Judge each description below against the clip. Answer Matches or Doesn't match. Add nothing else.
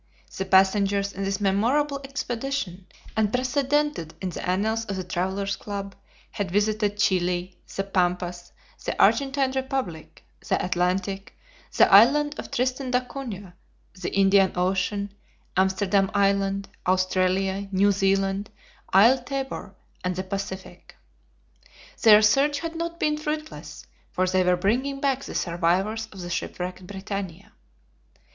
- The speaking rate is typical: Doesn't match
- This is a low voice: Doesn't match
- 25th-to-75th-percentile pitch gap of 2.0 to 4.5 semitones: Doesn't match